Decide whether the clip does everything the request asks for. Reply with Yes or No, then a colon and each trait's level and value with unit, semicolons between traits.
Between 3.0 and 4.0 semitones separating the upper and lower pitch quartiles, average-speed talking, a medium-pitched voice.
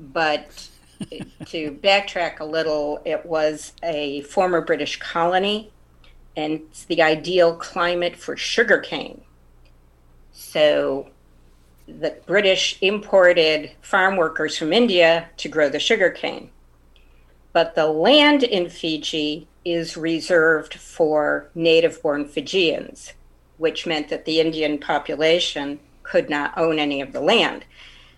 No: average, 3.3 semitones; slow, 115 wpm; medium, 155 Hz